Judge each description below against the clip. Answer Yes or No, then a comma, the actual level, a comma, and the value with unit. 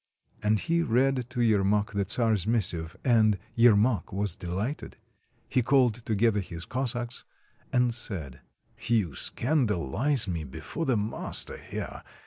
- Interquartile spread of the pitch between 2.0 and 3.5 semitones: No, average, 4.0 semitones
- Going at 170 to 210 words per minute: No, slow, 135 wpm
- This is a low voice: Yes, low, 110 Hz